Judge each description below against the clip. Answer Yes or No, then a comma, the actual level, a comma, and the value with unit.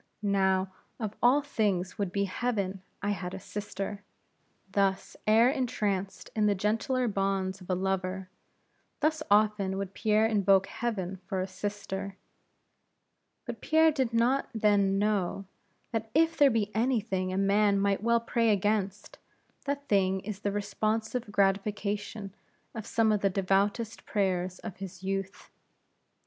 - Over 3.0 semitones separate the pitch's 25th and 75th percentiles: No, narrow, 2.4 semitones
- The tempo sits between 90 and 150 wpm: Yes, average, 145 wpm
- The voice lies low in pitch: No, high, 205 Hz